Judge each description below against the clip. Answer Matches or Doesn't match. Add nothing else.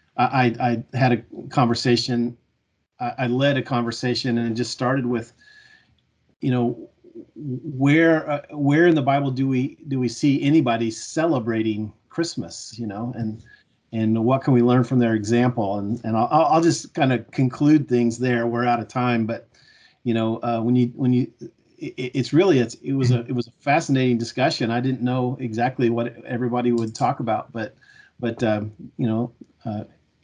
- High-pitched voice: Doesn't match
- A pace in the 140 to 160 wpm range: Doesn't match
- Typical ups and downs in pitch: Doesn't match